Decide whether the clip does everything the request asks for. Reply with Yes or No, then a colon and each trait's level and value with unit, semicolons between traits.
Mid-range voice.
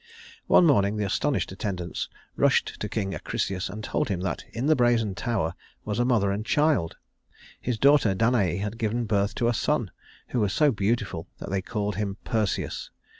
No: low, 105 Hz